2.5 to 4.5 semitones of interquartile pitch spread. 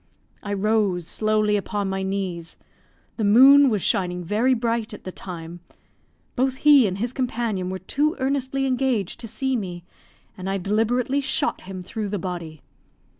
No: average, 5.2 semitones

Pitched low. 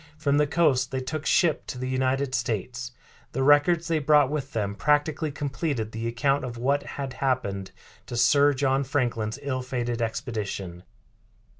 Yes: low, 130 Hz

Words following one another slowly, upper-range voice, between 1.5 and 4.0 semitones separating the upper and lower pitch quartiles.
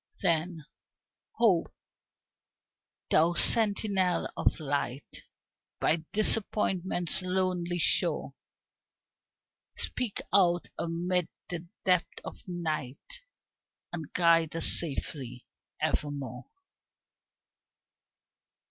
No: slow, 70 wpm; medium, 175 Hz; average, 2.8 semitones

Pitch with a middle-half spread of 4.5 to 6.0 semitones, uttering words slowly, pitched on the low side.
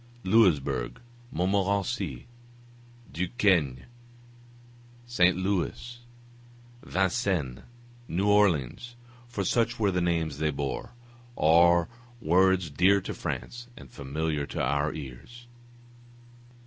Yes: average, 5.0 semitones; slow, 90 wpm; very low, 90 Hz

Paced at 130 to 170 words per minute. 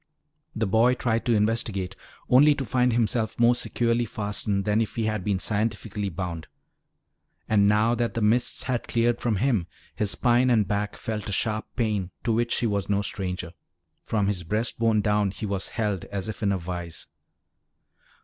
No: average, 180 wpm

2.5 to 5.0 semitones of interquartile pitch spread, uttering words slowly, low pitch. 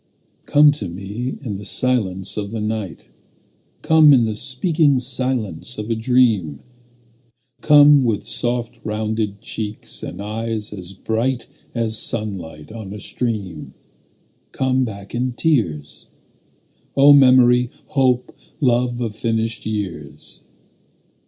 Yes: average, 3.6 semitones; slow, 120 wpm; low, 115 Hz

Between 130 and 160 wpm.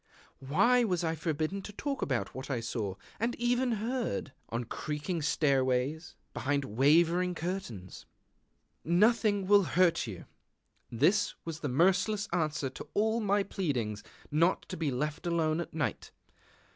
Yes: average, 140 wpm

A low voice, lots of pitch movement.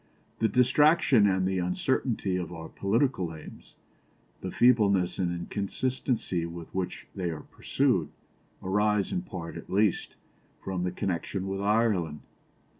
No: very low, 95 Hz; average, 4.0 semitones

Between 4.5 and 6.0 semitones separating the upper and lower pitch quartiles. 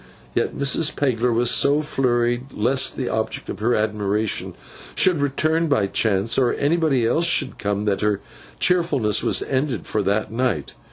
Yes: average, 4.8 semitones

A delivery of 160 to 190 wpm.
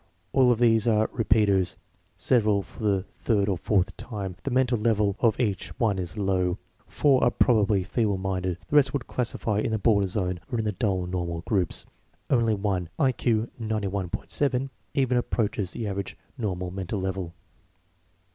Yes: average, 165 wpm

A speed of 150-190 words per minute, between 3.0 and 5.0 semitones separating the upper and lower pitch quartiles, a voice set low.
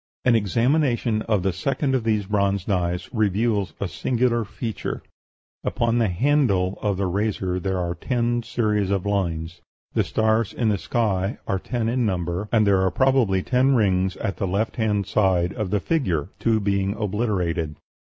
Yes: average, 170 wpm; average, 3.7 semitones; low, 105 Hz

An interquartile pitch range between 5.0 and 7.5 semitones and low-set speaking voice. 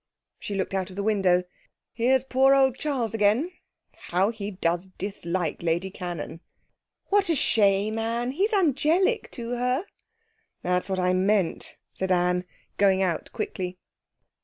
No: wide, 5.6 semitones; high, 205 Hz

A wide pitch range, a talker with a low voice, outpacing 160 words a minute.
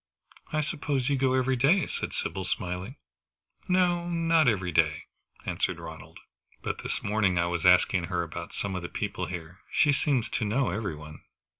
Yes: wide, 8.1 semitones; low, 105 Hz; average, 175 wpm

